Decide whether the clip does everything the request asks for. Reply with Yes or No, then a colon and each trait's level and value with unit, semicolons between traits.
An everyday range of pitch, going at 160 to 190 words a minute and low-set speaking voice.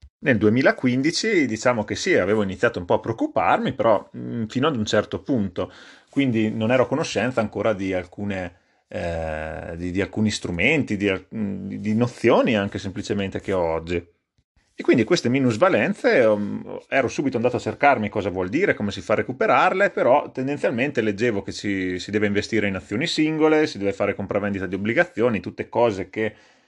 Yes: average, 3.3 semitones; fast, 170 wpm; low, 105 Hz